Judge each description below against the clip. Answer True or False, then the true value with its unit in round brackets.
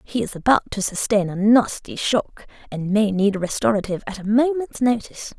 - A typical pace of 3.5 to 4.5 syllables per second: False (5.5 syllables/s)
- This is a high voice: True (215 Hz)